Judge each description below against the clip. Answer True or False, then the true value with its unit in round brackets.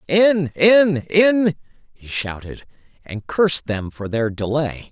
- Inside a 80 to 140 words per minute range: True (135 wpm)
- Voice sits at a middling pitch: True (150 Hz)